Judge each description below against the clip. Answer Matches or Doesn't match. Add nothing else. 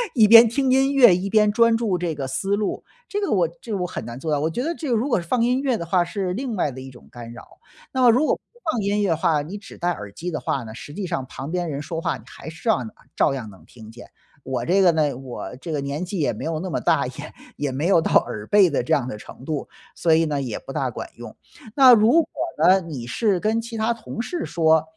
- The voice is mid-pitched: Matches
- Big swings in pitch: Matches